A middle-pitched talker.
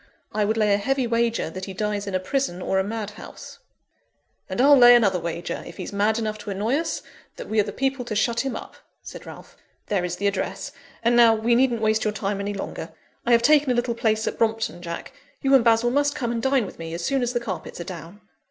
No: high, 220 Hz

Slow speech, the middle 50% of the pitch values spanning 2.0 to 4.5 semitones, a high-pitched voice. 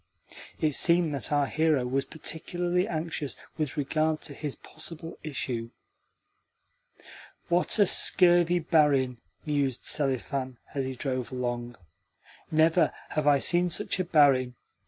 No: slow, 125 wpm; average, 3.7 semitones; medium, 150 Hz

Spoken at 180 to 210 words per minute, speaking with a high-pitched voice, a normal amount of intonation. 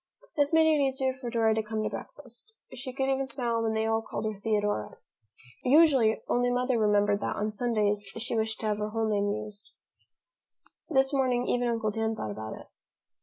Yes: average, 195 wpm; high, 225 Hz; average, 3.4 semitones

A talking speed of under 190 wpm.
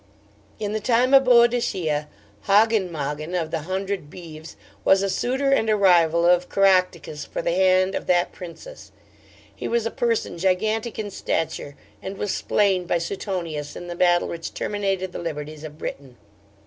Yes: average, 165 wpm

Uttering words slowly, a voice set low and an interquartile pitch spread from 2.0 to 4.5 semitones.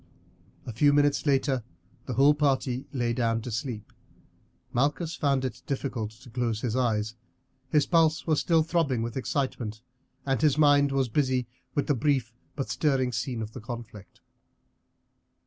No: average, 155 wpm; low, 130 Hz; average, 3.4 semitones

